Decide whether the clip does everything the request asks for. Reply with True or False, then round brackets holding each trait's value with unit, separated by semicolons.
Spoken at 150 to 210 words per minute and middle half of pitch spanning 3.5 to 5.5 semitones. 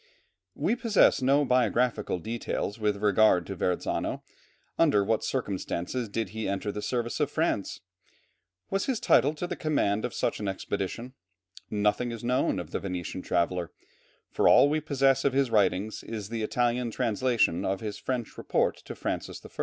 True (165 wpm; 4.5 semitones)